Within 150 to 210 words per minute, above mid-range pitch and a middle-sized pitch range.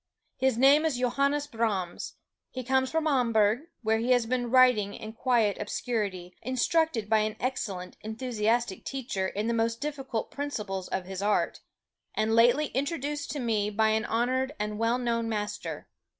Yes: average, 160 wpm; high, 230 Hz; average, 3.6 semitones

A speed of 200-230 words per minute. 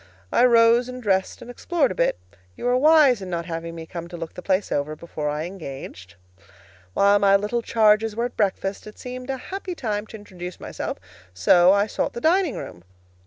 Yes: fast, 205 wpm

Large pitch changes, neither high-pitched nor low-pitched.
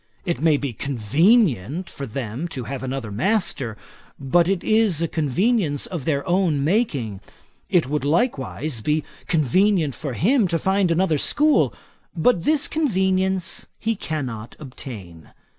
Yes: wide, 6.1 semitones; medium, 160 Hz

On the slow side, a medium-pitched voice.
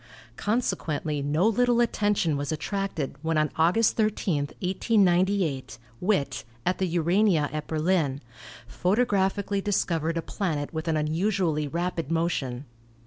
Yes: slow, 120 wpm; medium, 170 Hz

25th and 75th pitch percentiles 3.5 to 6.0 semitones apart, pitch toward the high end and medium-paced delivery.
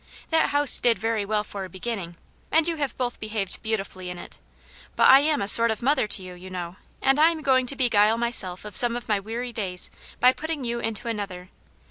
No: average, 4.7 semitones; high, 225 Hz; fast, 225 wpm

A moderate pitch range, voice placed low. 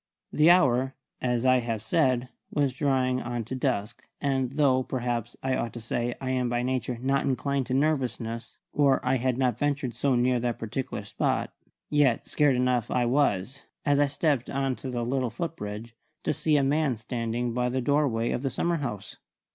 No: narrow, 2.3 semitones; low, 130 Hz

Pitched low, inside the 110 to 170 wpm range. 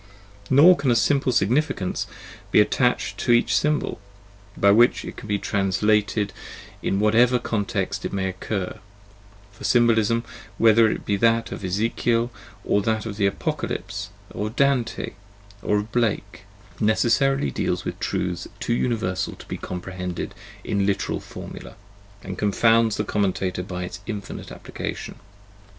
Yes: low, 105 Hz; average, 140 wpm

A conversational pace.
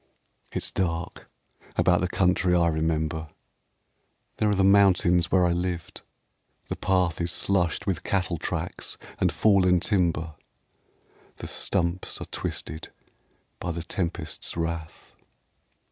No: slow, 120 wpm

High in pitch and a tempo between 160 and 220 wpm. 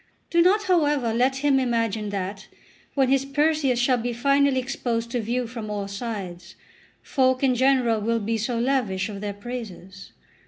Yes: high, 240 Hz; average, 165 wpm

